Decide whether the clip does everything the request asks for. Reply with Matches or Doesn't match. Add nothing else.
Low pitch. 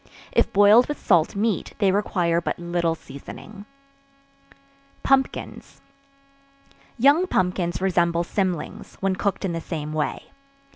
Doesn't match